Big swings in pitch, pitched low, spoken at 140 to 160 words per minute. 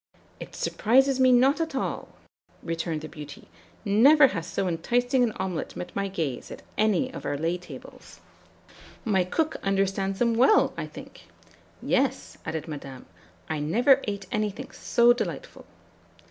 No: wide, 6.8 semitones; high, 200 Hz; average, 145 wpm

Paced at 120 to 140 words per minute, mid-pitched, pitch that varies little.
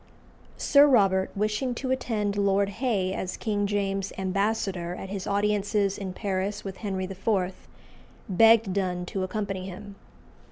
No: slow, 135 wpm; high, 200 Hz; narrow, 1.8 semitones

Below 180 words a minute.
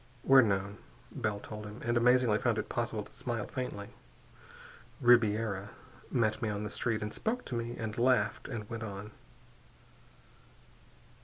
Yes: average, 155 wpm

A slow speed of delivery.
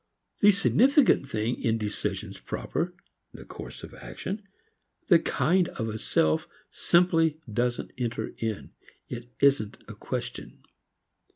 Yes: slow, 120 wpm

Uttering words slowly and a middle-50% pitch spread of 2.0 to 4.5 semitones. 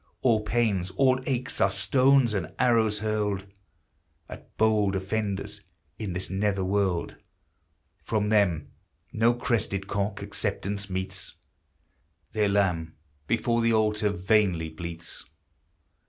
Yes: slow, 110 wpm; narrow, 2.5 semitones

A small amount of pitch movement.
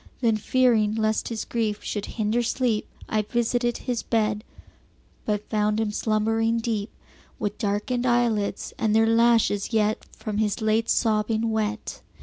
Yes: narrow, 1.5 semitones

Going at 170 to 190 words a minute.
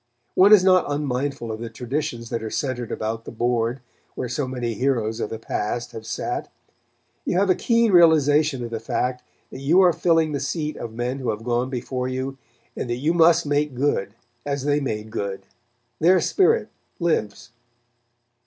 Yes: average, 180 wpm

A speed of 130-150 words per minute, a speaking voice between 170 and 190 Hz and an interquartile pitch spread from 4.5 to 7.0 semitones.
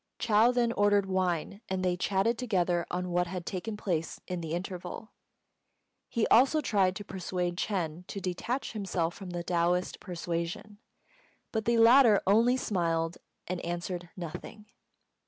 No: average, 145 wpm; medium, 185 Hz; average, 3.4 semitones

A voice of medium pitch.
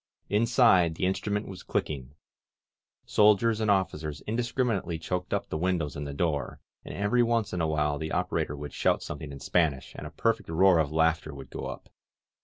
No: very low, 85 Hz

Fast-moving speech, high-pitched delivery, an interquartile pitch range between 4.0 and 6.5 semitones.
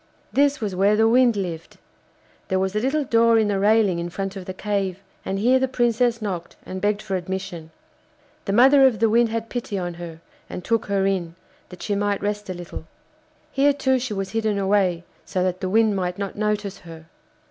No: fast, 210 wpm; high, 205 Hz; average, 3.4 semitones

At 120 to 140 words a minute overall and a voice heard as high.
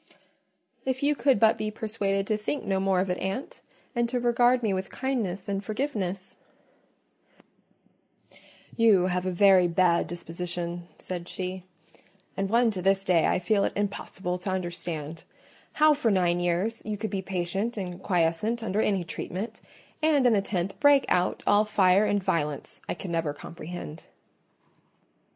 No: average, 160 wpm; high, 195 Hz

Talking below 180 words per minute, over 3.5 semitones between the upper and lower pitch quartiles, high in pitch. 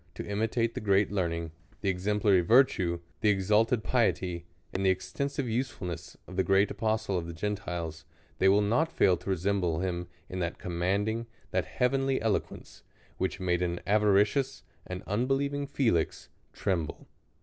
No: average, 160 wpm; average, 3.9 semitones; low, 100 Hz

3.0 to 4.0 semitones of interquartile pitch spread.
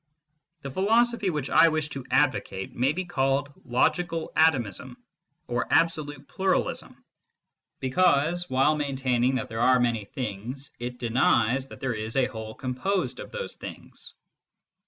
No: average, 4.5 semitones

